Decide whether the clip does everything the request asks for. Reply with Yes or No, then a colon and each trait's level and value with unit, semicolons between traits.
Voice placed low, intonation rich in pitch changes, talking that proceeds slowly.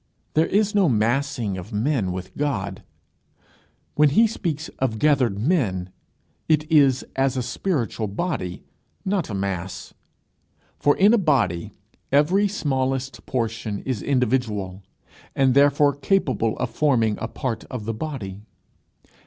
Yes: low, 130 Hz; wide, 5.8 semitones; slow, 130 wpm